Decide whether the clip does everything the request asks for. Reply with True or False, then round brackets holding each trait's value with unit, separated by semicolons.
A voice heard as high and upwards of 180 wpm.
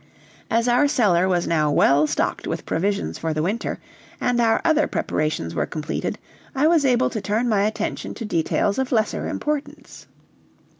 False (215 Hz; 165 wpm)